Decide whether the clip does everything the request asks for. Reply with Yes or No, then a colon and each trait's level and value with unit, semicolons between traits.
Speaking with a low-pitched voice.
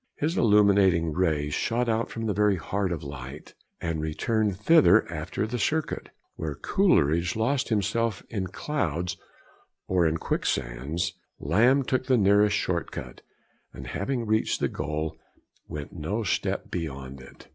Yes: very low, 95 Hz